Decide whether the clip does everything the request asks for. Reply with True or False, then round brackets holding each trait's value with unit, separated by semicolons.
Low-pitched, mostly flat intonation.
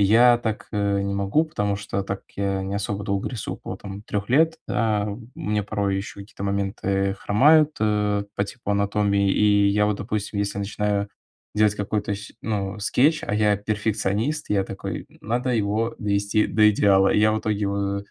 True (105 Hz; 1.4 semitones)